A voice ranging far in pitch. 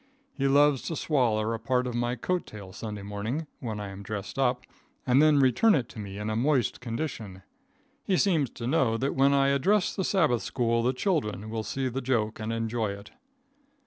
No: average, 4.2 semitones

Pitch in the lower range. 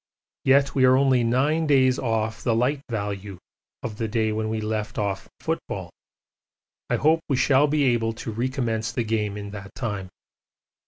Yes: low, 115 Hz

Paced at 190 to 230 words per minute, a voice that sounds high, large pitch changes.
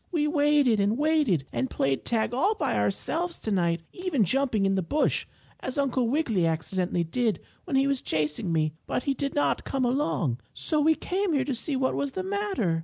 Yes: average, 195 wpm; very high, 255 Hz; wide, 8.6 semitones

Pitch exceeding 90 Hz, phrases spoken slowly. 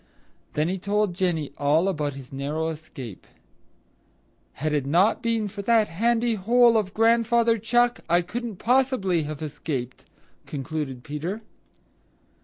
Yes: medium, 185 Hz; slow, 130 wpm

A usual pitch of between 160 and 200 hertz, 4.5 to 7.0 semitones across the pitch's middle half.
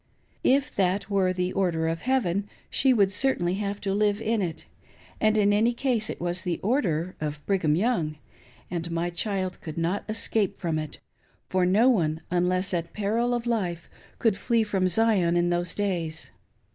No: high, 190 Hz; average, 3.8 semitones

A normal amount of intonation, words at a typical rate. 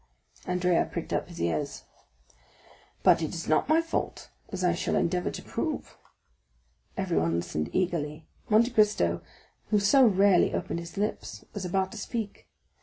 Yes: average, 4.9 semitones; average, 150 wpm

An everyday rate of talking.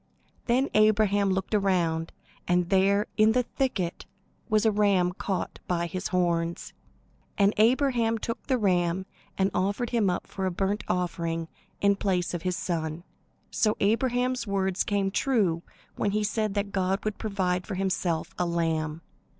Yes: average, 155 wpm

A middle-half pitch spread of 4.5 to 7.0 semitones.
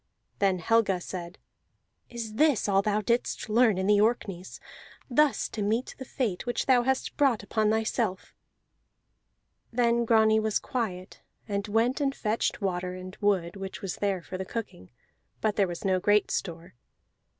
No: average, 3.7 semitones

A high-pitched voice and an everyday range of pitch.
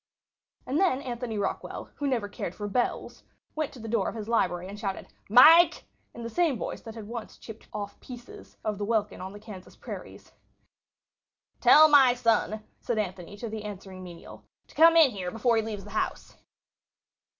Yes: high, 220 Hz; average, 3.4 semitones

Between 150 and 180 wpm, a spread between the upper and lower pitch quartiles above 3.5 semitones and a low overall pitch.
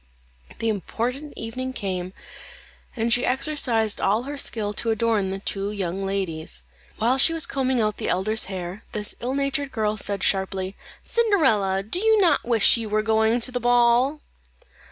No: average, 165 wpm; average, 4.6 semitones; high, 225 Hz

